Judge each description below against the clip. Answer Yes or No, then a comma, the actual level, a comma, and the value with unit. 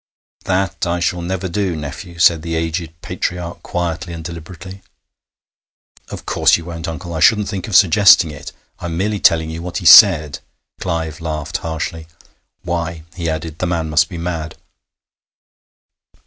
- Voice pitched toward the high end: No, very low, 85 Hz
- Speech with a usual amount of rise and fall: No, narrow, 1.8 semitones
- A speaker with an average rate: Yes, average, 160 wpm